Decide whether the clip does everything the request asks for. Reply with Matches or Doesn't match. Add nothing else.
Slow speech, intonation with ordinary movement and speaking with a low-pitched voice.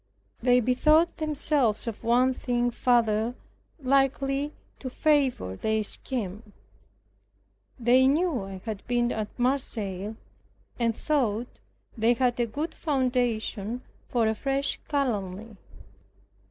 Doesn't match